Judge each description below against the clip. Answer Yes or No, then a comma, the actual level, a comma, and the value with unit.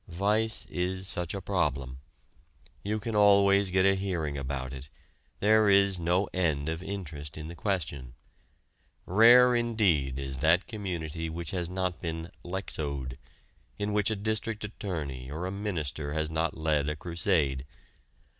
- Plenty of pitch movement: No, average, 4.8 semitones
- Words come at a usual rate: Yes, average, 145 wpm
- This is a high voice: No, very low, 90 Hz